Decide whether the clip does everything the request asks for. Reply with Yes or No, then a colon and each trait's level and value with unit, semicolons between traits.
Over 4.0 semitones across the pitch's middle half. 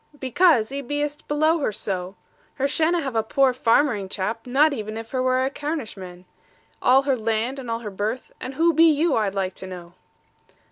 Yes: average, 5.1 semitones